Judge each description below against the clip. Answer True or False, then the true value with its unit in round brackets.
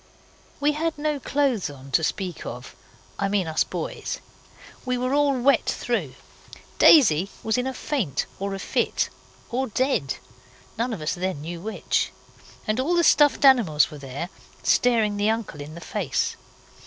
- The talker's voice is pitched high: True (220 Hz)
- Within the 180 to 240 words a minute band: False (165 wpm)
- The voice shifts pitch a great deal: True (7.7 semitones)